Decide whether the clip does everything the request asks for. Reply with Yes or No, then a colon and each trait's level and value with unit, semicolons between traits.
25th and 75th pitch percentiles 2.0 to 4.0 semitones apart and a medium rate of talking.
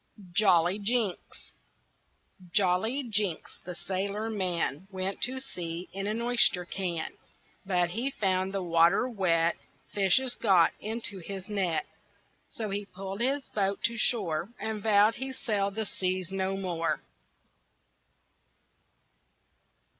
No: average, 3.2 semitones; slow, 120 wpm